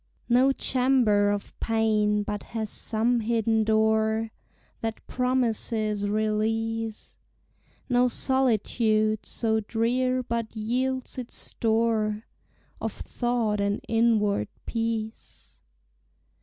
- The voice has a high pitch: Yes, high, 225 Hz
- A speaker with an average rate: No, slow, 90 wpm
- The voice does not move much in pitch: Yes, narrow, 1.8 semitones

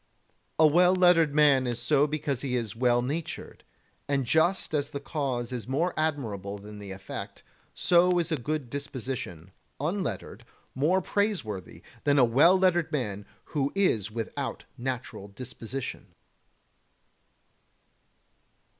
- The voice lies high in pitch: No, medium, 140 Hz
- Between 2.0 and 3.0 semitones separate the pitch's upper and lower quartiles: No, average, 5.1 semitones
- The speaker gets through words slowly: Yes, slow, 130 wpm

